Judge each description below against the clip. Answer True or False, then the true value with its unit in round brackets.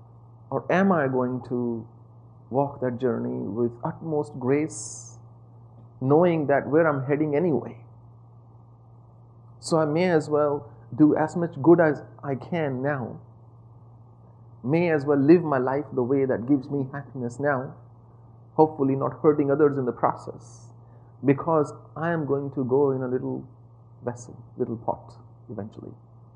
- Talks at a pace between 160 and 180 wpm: False (145 wpm)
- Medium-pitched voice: False (125 Hz)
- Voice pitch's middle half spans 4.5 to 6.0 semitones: False (3.8 semitones)